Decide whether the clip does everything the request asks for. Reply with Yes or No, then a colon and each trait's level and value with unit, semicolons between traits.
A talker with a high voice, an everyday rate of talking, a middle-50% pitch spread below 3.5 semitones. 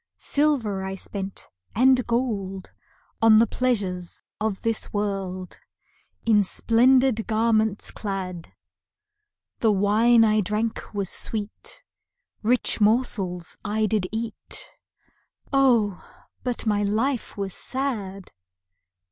No: high, 215 Hz; slow, 100 wpm; average, 2.9 semitones